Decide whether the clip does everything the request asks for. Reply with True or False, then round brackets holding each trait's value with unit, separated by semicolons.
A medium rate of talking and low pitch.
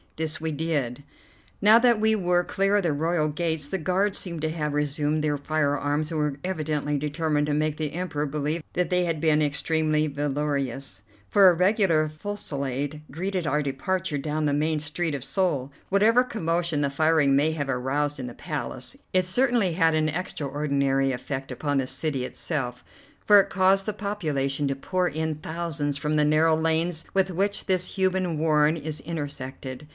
False (175 wpm; 155 Hz)